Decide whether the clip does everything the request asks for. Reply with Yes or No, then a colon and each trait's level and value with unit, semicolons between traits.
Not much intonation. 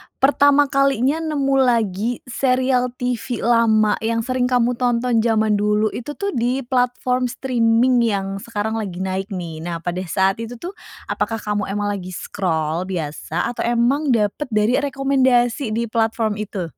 No: average, 3.5 semitones